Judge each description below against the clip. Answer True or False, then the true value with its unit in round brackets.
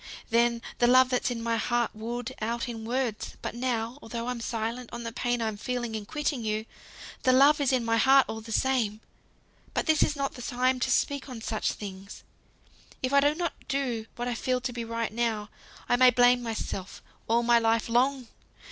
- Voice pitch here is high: True (240 Hz)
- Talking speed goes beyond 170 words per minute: True (205 wpm)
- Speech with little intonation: True (2.1 semitones)